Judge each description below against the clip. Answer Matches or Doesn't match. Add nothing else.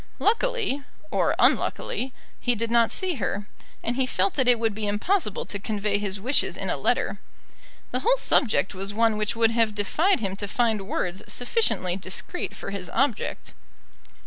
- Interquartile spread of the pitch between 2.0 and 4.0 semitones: Doesn't match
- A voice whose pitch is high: Matches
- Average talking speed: Matches